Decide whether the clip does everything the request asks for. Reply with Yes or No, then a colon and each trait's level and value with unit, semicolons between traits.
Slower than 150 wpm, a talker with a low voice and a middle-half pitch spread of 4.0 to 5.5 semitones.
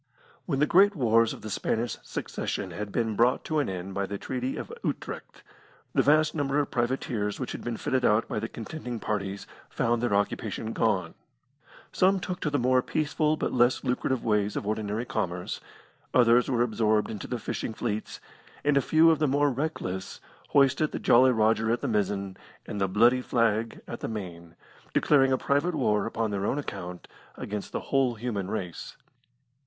No: average, 185 wpm; low, 115 Hz; average, 4.4 semitones